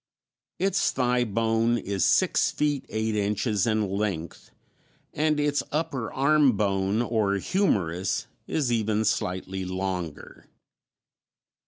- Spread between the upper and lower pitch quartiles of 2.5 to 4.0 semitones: No, average, 5.1 semitones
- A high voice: No, low, 110 Hz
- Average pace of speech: No, slow, 110 wpm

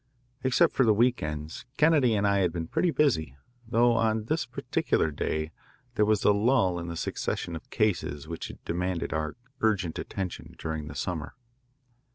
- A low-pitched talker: Yes, very low, 95 Hz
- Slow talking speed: No, average, 175 wpm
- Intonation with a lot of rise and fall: Yes, wide, 6.3 semitones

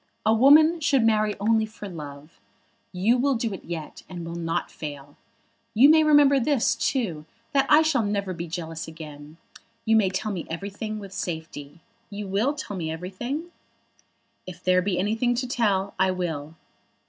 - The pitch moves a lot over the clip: Yes, wide, 6.3 semitones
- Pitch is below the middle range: No, high, 200 Hz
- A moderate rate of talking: Yes, average, 170 wpm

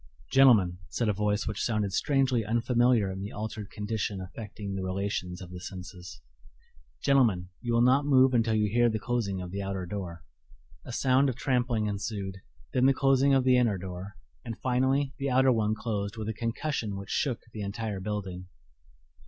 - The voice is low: Yes, low, 110 Hz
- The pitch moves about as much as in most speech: Yes, average, 4.2 semitones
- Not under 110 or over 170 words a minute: No, average, 180 wpm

